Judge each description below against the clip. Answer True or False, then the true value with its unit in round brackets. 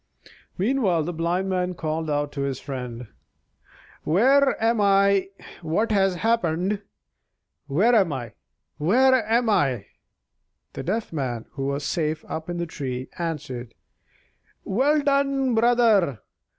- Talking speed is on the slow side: True (125 wpm)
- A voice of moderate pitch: True (175 Hz)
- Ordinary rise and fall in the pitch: False (7.5 semitones)